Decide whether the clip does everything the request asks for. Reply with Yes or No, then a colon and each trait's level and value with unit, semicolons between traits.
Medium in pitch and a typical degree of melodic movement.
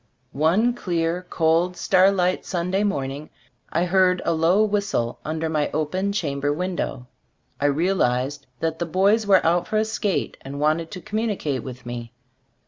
Yes: medium, 170 Hz; average, 4.5 semitones